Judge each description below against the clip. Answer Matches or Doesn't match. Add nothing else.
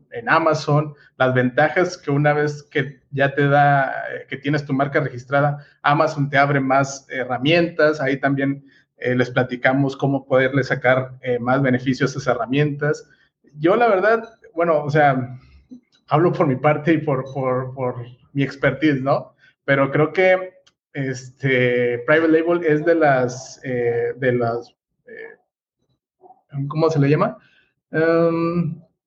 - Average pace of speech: Matches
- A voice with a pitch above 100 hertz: Matches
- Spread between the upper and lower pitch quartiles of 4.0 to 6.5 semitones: Doesn't match